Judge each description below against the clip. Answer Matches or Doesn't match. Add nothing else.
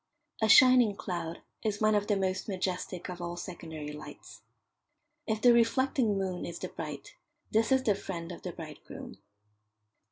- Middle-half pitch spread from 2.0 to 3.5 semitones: Doesn't match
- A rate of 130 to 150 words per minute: Doesn't match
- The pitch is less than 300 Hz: Matches